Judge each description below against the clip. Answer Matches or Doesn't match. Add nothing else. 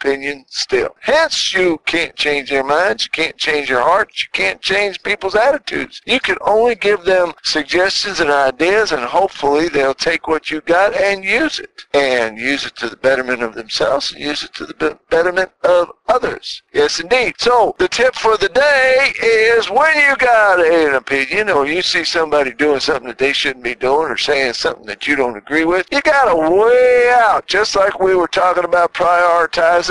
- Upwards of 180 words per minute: Matches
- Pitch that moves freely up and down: Matches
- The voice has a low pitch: Doesn't match